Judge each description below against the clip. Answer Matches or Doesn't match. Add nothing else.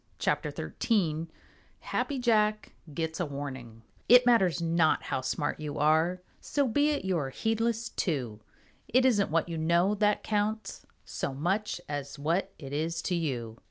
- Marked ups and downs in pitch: Matches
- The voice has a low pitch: Doesn't match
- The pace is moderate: Matches